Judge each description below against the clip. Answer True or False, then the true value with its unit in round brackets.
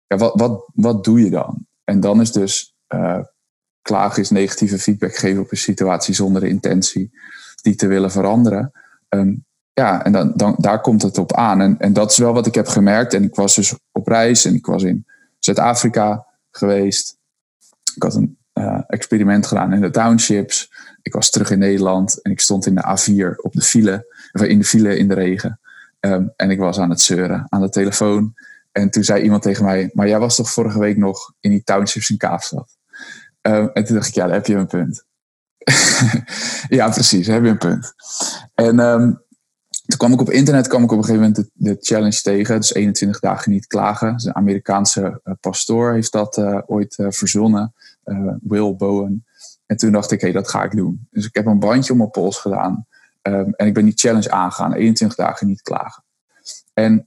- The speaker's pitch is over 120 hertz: False (105 Hz)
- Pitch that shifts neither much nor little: False (2.2 semitones)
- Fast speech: True (210 wpm)